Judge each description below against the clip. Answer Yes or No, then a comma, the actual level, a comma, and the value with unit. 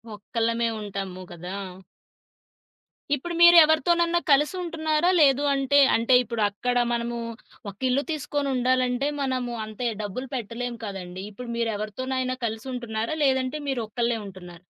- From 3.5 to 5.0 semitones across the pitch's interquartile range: Yes, average, 4.1 semitones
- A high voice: Yes, high, 245 Hz